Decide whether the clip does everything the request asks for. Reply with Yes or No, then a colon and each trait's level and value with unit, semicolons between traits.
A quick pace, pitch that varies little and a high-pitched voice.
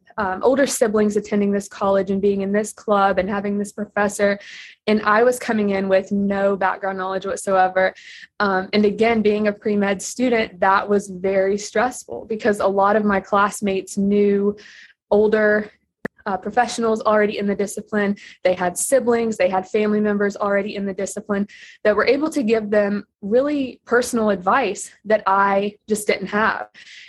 No: average, 170 wpm; narrow, 1.5 semitones; high, 205 Hz